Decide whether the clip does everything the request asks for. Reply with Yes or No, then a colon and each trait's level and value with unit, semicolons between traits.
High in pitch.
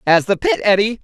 Yes: high, 210 Hz